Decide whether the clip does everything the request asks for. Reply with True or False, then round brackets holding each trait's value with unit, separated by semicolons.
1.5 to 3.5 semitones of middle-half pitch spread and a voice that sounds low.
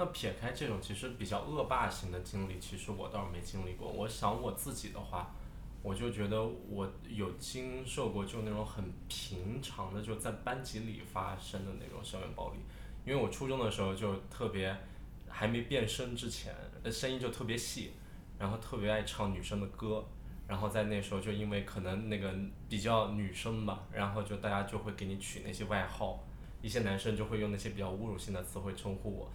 True (2.4 semitones; 105 Hz)